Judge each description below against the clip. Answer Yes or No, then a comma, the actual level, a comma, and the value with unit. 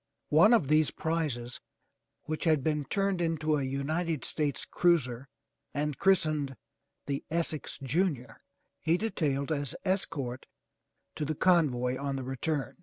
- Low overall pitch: No, medium, 150 Hz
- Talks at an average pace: No, slow, 130 wpm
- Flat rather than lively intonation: No, average, 3.3 semitones